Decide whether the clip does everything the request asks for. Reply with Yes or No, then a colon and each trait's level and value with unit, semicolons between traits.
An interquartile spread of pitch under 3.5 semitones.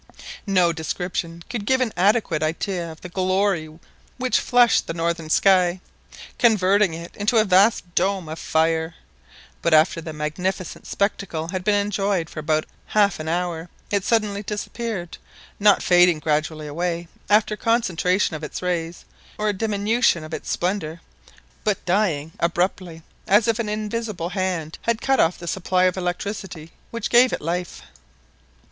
No: average, 3.8 semitones